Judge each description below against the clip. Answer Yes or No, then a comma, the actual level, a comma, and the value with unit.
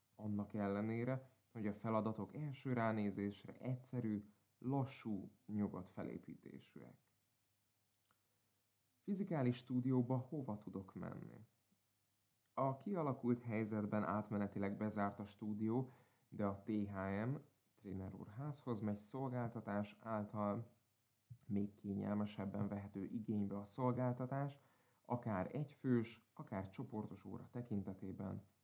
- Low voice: Yes, low, 110 Hz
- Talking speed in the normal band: No, slow, 90 wpm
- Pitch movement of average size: Yes, average, 3.5 semitones